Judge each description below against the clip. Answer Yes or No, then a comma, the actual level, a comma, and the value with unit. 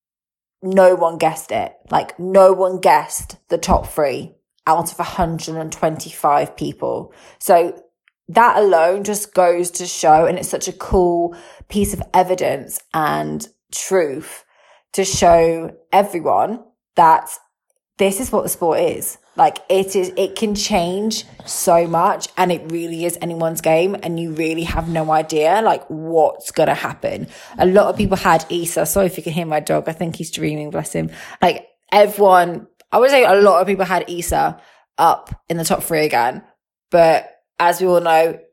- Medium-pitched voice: Yes, medium, 175 Hz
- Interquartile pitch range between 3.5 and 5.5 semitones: No, average, 2.8 semitones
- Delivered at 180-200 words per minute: No, average, 170 wpm